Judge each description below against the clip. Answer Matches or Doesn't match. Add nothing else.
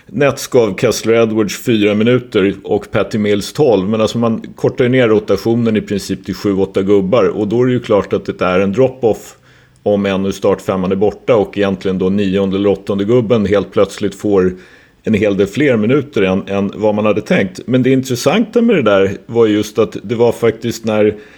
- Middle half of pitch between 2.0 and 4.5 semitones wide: Matches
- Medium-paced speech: Doesn't match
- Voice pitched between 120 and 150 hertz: Doesn't match